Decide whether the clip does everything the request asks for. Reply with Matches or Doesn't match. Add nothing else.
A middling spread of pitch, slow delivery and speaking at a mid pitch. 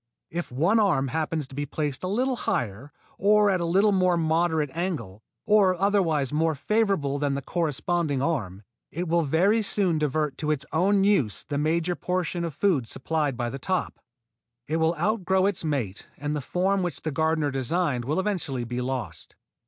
Doesn't match